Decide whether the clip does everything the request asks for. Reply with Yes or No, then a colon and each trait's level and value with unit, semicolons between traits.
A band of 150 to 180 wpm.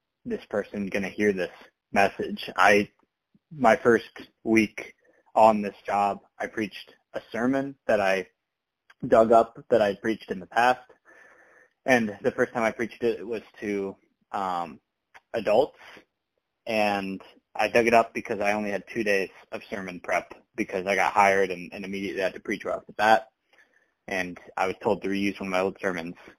Yes: average, 175 wpm